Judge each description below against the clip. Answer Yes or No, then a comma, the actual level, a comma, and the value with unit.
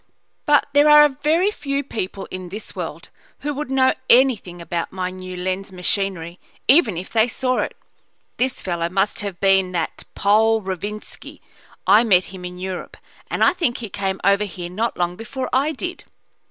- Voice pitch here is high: Yes, high, 200 Hz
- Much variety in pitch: Yes, wide, 6.0 semitones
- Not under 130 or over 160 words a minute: No, average, 175 wpm